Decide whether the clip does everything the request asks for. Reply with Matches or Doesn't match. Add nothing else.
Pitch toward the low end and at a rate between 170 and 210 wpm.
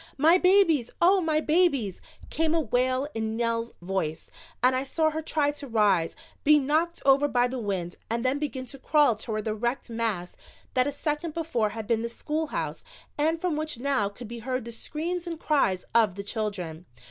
Doesn't match